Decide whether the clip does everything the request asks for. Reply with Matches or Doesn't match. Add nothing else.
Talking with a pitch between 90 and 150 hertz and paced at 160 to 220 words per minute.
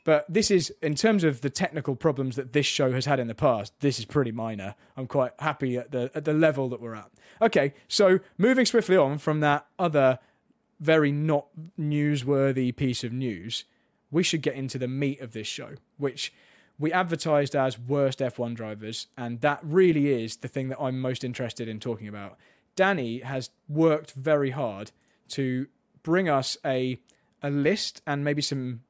Matches